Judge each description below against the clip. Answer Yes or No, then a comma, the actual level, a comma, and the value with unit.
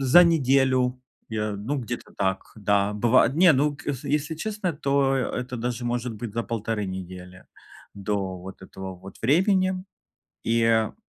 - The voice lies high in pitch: No, low, 120 Hz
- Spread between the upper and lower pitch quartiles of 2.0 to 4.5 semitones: No, wide, 5.5 semitones